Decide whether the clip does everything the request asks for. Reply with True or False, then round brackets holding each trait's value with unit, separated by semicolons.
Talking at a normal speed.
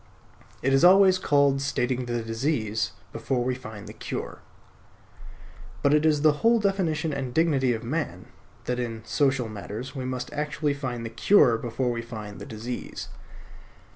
True (160 wpm)